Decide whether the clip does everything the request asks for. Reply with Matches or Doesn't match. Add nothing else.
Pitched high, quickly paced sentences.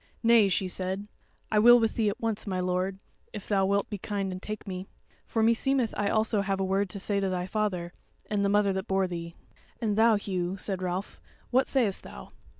Matches